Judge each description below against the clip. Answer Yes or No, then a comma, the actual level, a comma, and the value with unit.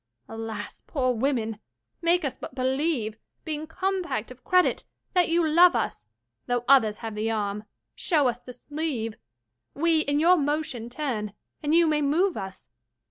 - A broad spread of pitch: Yes, wide, 6.1 semitones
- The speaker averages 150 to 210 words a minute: Yes, average, 160 wpm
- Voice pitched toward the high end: Yes, very high, 275 Hz